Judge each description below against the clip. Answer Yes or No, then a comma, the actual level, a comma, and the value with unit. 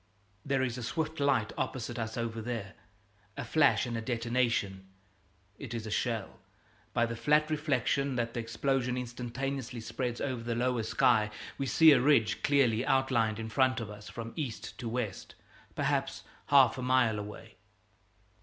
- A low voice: Yes, low, 120 Hz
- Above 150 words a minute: Yes, average, 165 wpm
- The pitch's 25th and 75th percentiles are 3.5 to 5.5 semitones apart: No, average, 2.8 semitones